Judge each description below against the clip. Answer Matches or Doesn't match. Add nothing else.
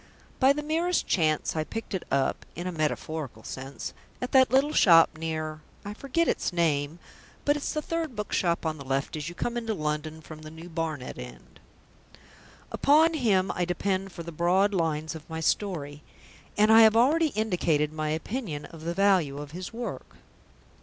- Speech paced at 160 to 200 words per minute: Matches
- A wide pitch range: Matches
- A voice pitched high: Doesn't match